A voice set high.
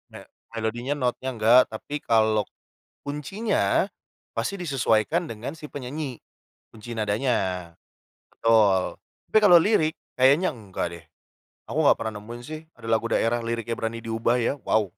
No: low, 115 Hz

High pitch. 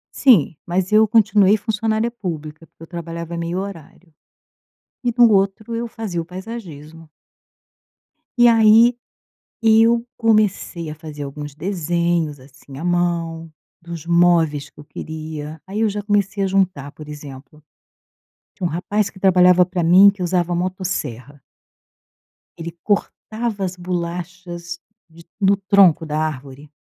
No: medium, 175 Hz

